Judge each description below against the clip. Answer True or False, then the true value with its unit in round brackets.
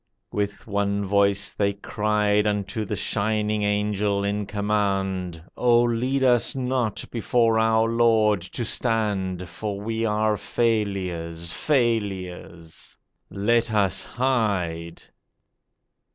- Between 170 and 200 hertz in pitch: False (105 Hz)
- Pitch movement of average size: False (2.3 semitones)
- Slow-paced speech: True (105 wpm)